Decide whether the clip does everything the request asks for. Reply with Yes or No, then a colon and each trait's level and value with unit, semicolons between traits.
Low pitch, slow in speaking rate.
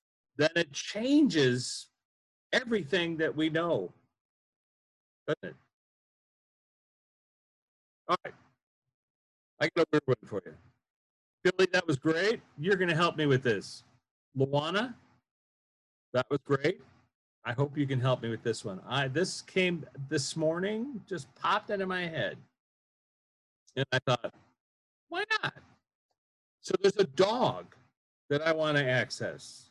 No: medium, 155 Hz; slow, 130 wpm